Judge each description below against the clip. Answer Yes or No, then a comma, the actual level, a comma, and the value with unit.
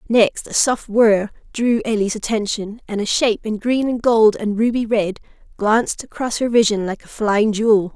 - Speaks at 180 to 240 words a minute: Yes, average, 190 wpm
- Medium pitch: No, high, 220 Hz